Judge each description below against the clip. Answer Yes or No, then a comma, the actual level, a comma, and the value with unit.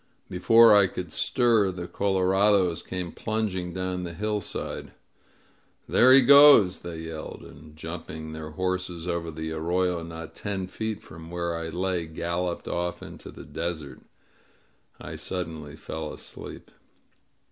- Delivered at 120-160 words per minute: Yes, slow, 135 wpm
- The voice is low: Yes, very low, 90 Hz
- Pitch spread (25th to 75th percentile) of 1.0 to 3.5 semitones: Yes, average, 2.7 semitones